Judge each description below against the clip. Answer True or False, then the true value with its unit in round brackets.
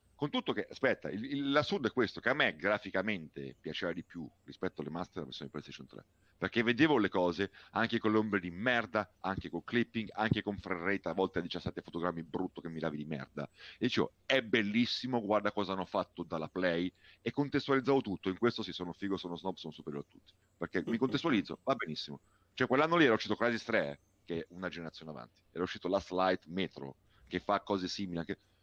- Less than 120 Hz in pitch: True (95 Hz)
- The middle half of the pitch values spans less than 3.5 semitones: False (4.1 semitones)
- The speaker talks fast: True (210 wpm)